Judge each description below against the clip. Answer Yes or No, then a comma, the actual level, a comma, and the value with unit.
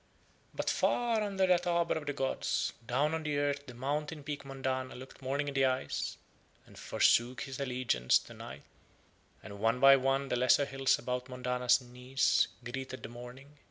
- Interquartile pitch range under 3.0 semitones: Yes, narrow, 2.4 semitones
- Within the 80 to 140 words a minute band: No, average, 175 wpm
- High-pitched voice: No, low, 135 Hz